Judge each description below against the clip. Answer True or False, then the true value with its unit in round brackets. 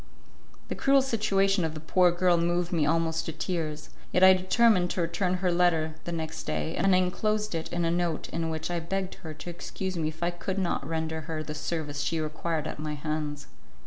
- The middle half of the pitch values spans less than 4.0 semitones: True (2.5 semitones)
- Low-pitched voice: False (170 Hz)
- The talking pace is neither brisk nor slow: False (215 wpm)